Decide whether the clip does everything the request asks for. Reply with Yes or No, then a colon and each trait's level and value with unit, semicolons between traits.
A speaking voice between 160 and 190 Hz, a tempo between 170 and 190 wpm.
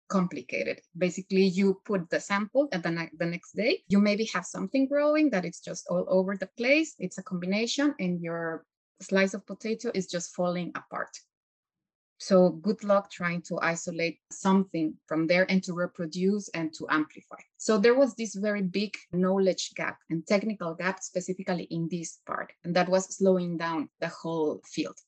Yes: medium, 185 Hz; average, 175 wpm